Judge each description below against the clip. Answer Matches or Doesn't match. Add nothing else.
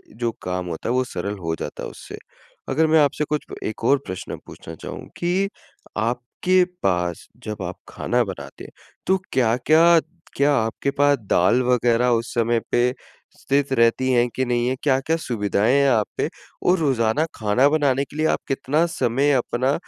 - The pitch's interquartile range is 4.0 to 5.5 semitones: Matches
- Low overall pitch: Matches